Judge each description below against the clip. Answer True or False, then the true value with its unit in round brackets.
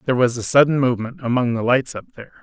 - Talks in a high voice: False (125 Hz)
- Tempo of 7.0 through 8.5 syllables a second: True (7.7 syllables/s)